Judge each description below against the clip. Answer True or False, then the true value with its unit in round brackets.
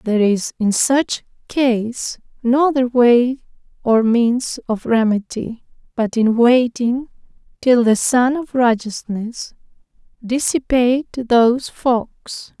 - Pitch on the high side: True (240 Hz)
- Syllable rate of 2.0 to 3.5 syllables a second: True (3.4 syllables/s)